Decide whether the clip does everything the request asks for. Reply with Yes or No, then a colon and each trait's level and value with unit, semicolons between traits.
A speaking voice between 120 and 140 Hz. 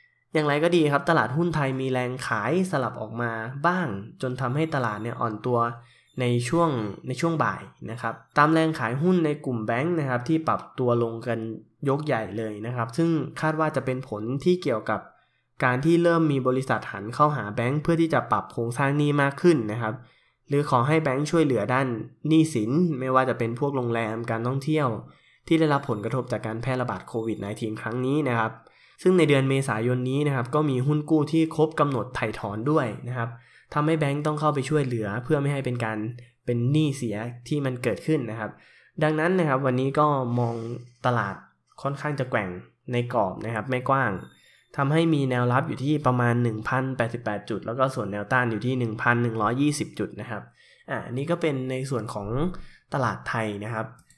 Yes: low, 130 Hz